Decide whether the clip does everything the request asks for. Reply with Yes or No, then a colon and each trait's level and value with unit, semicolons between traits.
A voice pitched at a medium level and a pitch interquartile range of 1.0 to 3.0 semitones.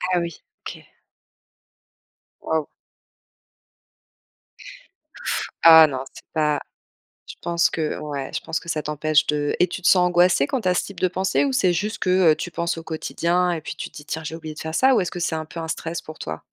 Yes: medium, 165 Hz; narrow, 2.5 semitones